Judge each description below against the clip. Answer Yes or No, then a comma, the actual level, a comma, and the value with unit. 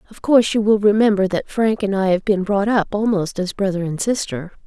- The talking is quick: Yes, fast, 230 wpm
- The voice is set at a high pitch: Yes, high, 200 Hz